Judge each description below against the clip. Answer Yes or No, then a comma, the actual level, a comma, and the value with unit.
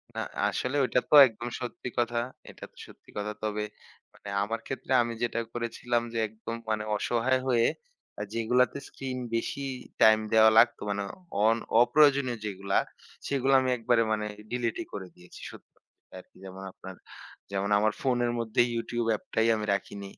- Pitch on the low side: Yes, low, 115 Hz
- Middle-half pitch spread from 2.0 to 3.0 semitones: Yes, narrow, 2.5 semitones